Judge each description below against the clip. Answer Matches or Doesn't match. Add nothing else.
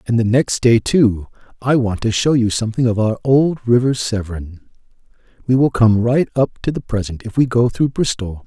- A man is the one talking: Matches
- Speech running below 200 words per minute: Doesn't match